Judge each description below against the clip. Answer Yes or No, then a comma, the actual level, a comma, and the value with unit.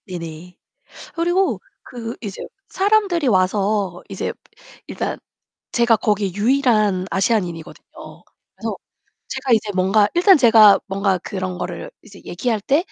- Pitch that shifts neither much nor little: Yes, average, 4.8 semitones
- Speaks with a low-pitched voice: No, high, 210 Hz